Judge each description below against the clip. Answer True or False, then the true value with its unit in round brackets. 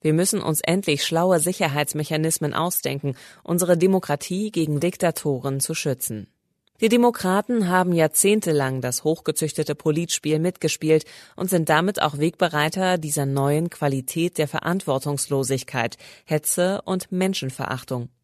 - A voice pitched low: False (155 Hz)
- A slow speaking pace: True (110 wpm)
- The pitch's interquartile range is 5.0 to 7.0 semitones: False (3.8 semitones)